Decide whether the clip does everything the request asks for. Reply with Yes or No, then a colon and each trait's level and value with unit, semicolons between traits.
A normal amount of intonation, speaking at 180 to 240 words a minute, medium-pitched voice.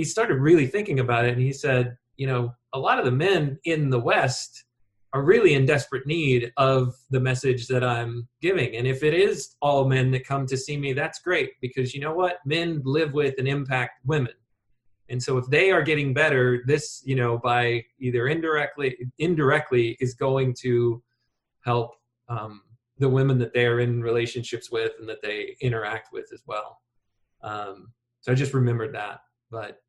No: average, 3.3 semitones; average, 190 wpm; low, 130 Hz